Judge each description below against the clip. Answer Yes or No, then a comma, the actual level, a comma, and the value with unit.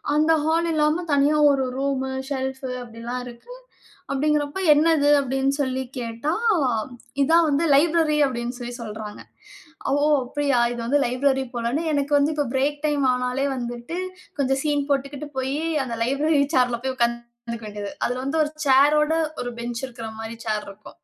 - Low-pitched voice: No, very high, 270 Hz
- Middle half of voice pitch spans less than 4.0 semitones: Yes, average, 3.4 semitones